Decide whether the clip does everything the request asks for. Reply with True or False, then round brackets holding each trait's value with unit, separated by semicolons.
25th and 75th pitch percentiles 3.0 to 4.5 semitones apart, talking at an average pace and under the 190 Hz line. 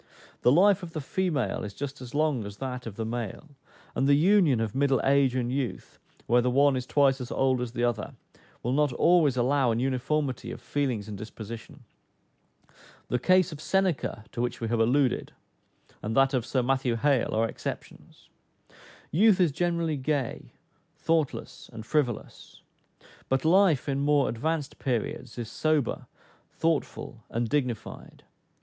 True (3.9 semitones; 160 wpm; 135 Hz)